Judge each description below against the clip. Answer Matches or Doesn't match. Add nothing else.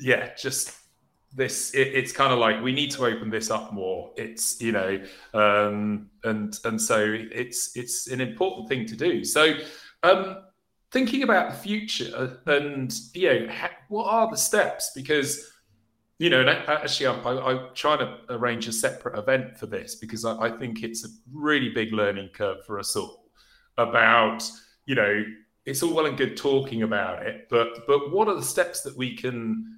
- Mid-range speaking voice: Doesn't match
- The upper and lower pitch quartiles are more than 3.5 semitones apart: Matches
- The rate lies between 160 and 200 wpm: Matches